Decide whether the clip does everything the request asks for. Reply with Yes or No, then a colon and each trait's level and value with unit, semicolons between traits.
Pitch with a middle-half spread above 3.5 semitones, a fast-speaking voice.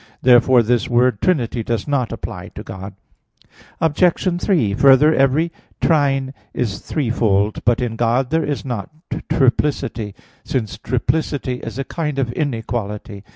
No: average, 4.1 semitones; slow, 135 wpm